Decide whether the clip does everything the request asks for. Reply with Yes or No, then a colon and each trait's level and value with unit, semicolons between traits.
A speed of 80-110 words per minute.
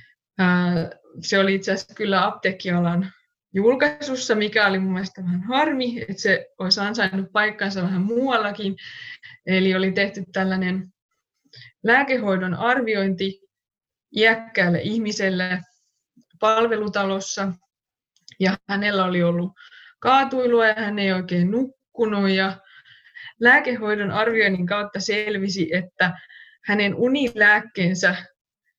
Yes: average, 100 wpm